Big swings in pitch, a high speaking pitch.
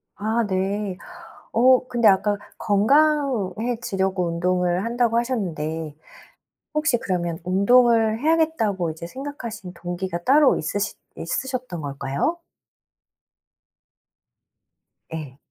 Yes: wide, 5.7 semitones; high, 205 Hz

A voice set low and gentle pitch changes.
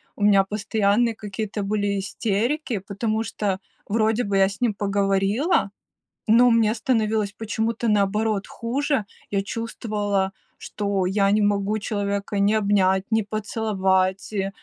No: high, 205 Hz; narrow, 1.9 semitones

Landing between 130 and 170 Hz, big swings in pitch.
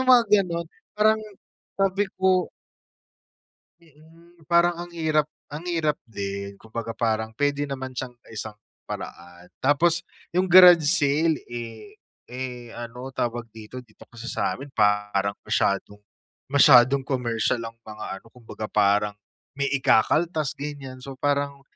Yes: low, 135 Hz; wide, 6.3 semitones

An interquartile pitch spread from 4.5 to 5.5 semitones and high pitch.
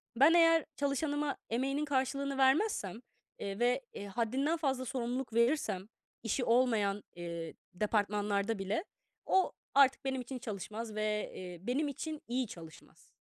Yes: average, 4.9 semitones; high, 245 Hz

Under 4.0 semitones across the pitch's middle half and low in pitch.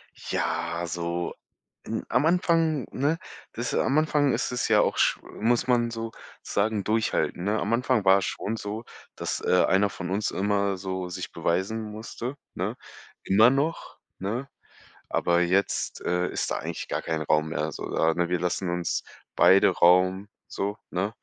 No: average, 4.6 semitones; low, 100 Hz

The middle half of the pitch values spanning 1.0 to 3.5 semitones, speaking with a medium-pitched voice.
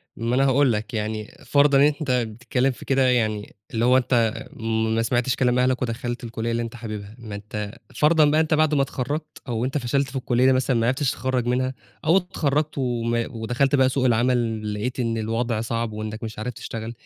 No: average, 2.8 semitones; low, 125 Hz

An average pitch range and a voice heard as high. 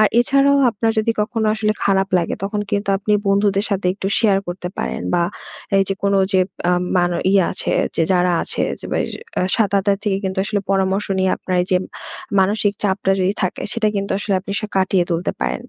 No: narrow, 1.9 semitones; high, 195 Hz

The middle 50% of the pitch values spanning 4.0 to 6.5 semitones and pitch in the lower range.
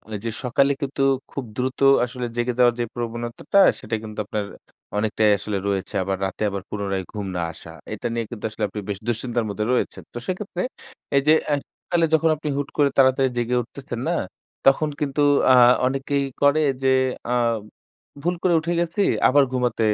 Yes: average, 4.5 semitones; low, 125 Hz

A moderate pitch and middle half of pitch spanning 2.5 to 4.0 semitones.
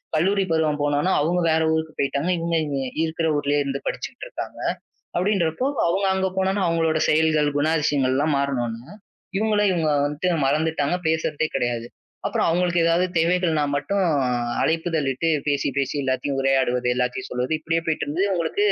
Yes: medium, 160 Hz; average, 3.3 semitones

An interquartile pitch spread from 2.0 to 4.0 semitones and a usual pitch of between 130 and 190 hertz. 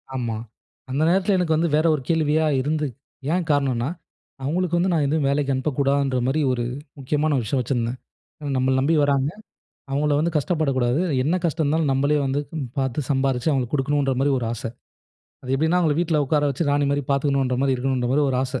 Yes: average, 2.7 semitones; medium, 140 Hz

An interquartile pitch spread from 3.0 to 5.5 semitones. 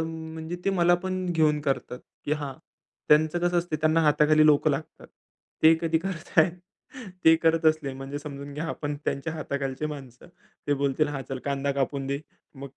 No: narrow, 2.5 semitones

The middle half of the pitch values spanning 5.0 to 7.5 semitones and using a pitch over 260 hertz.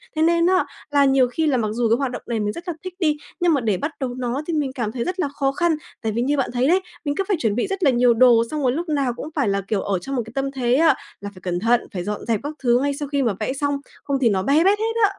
No: average, 4.4 semitones; very high, 270 Hz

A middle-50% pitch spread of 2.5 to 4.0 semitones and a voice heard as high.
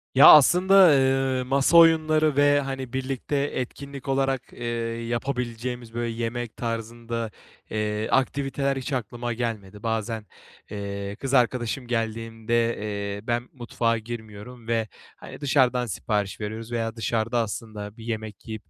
No: average, 3.1 semitones; low, 120 Hz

